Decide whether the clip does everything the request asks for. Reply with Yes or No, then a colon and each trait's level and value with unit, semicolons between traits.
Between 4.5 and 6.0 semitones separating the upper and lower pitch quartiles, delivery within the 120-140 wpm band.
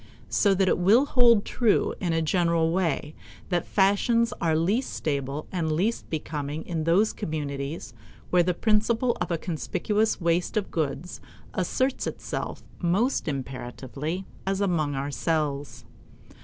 Yes: average, 4.9 semitones; slow, 135 wpm